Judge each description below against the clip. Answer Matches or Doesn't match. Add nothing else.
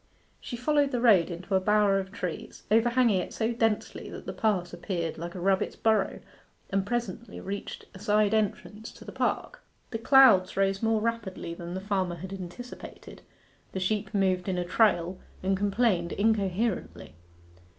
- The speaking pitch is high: Matches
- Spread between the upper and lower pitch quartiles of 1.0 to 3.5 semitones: Matches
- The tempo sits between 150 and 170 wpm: Matches